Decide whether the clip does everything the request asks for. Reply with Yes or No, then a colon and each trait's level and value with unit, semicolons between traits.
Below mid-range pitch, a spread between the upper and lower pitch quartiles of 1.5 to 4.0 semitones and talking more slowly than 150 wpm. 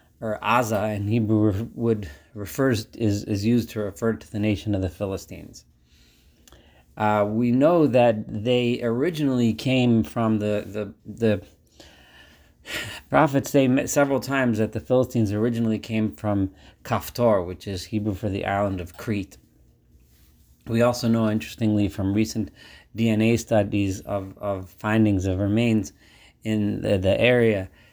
Yes: low, 105 Hz; average, 2.7 semitones; average, 140 wpm